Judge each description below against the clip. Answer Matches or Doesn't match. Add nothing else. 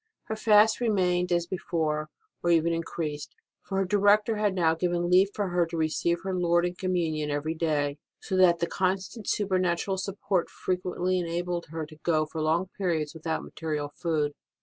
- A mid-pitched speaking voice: Matches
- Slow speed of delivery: Doesn't match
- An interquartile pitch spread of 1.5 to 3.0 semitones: Matches